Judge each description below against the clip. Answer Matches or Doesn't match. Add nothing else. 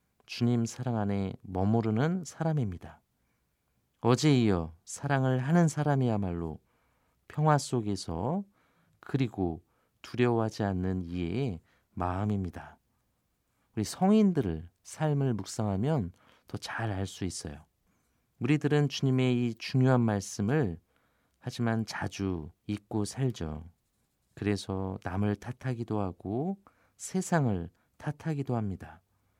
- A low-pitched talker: Matches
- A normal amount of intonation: Doesn't match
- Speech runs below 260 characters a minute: Matches